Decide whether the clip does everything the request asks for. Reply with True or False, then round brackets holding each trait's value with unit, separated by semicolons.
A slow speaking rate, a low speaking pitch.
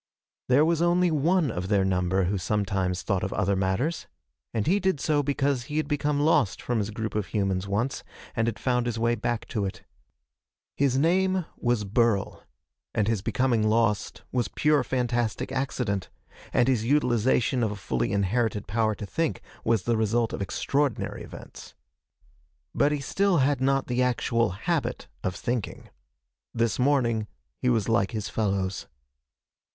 False (165 wpm; 115 Hz)